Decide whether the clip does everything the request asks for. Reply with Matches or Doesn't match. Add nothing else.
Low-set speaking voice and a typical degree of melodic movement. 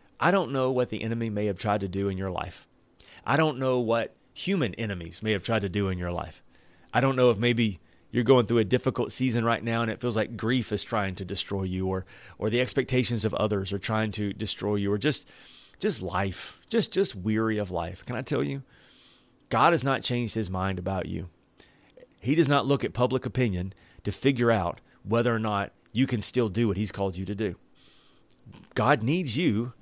Matches